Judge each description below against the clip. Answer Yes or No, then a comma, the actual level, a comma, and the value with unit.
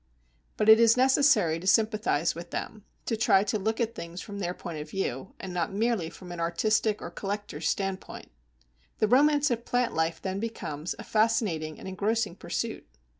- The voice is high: Yes, high, 200 Hz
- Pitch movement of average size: Yes, average, 4.6 semitones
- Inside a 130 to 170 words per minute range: No, average, 180 wpm